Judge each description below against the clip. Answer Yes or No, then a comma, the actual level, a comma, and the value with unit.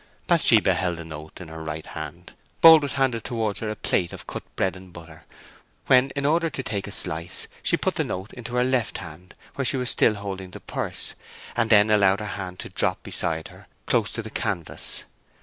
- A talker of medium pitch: No, low, 105 Hz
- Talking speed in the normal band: No, fast, 210 wpm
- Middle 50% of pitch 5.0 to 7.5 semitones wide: Yes, wide, 5.5 semitones